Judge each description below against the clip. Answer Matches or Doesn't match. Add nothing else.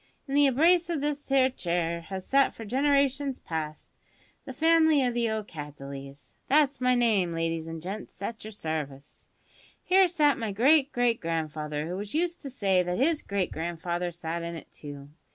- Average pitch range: Doesn't match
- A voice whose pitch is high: Matches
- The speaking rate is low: Doesn't match